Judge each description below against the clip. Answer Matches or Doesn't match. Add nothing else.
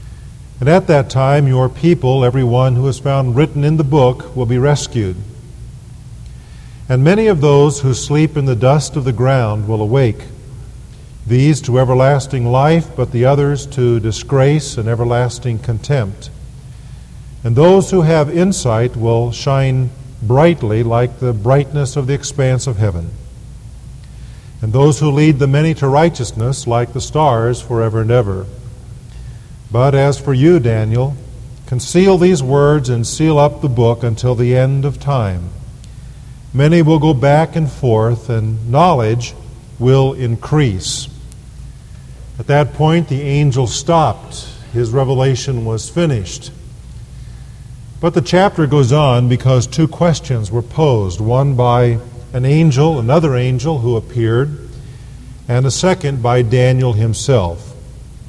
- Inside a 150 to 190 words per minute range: Doesn't match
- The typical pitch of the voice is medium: Doesn't match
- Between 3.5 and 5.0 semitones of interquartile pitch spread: Doesn't match